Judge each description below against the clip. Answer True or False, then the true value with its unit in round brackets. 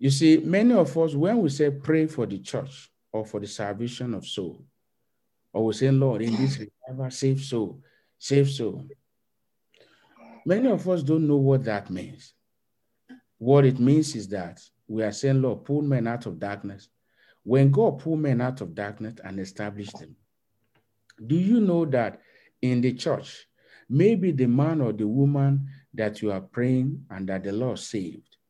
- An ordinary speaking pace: True (175 wpm)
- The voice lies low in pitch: True (130 Hz)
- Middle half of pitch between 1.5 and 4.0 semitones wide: False (4.5 semitones)